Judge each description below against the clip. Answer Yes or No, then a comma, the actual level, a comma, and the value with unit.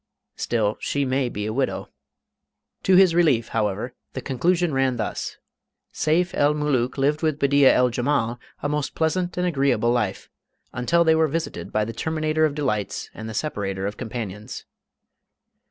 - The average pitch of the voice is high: No, low, 135 Hz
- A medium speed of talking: Yes, average, 160 wpm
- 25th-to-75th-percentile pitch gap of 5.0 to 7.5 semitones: Yes, average, 5.3 semitones